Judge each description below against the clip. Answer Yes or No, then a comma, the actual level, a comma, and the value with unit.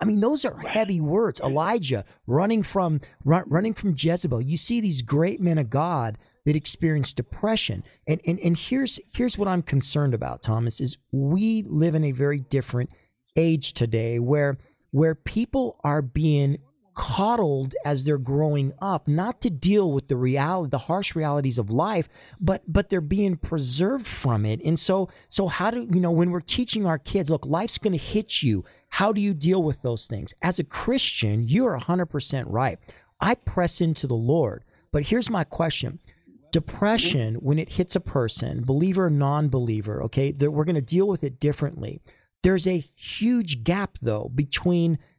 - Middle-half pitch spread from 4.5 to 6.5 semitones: Yes, wide, 5.4 semitones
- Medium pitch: Yes, medium, 160 Hz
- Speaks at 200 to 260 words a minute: No, average, 175 wpm